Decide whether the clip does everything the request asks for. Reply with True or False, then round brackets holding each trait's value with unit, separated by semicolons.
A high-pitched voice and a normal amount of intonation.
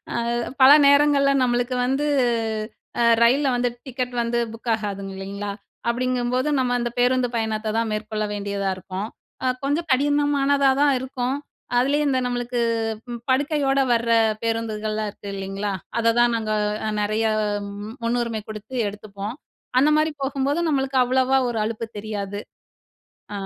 True (240 Hz; 3.8 semitones)